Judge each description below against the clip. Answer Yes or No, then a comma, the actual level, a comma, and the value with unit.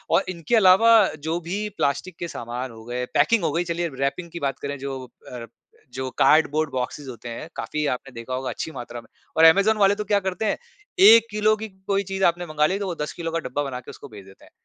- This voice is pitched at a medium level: Yes, medium, 160 Hz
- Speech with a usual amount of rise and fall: No, wide, 6.5 semitones